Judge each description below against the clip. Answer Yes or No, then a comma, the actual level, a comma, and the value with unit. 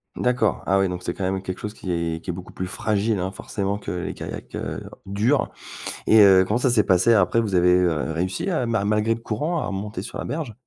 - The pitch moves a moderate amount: Yes, average, 3.6 semitones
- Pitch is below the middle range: Yes, low, 100 Hz